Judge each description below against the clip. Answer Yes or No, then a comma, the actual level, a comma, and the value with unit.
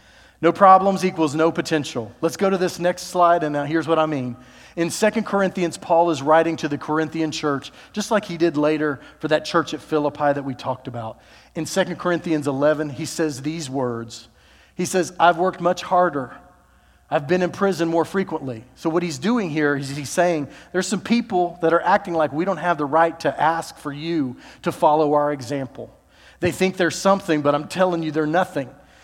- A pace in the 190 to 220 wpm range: Yes, fast, 205 wpm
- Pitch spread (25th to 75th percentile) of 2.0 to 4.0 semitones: Yes, average, 3.3 semitones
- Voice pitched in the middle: Yes, medium, 160 Hz